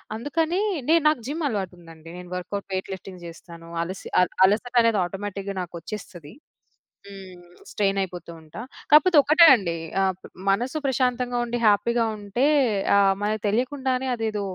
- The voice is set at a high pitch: Yes, high, 205 Hz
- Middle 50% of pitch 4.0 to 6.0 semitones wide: Yes, wide, 5.4 semitones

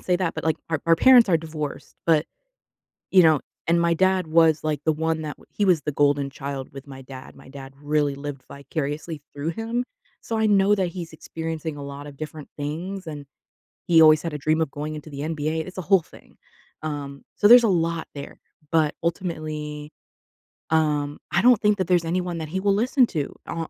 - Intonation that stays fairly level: No, average, 3.3 semitones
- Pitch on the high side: No, medium, 160 Hz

